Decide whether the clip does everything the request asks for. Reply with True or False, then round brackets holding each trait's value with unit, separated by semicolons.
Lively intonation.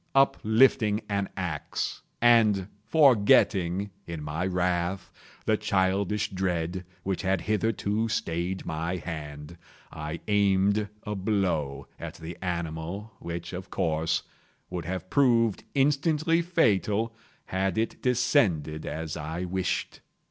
False (4.0 semitones)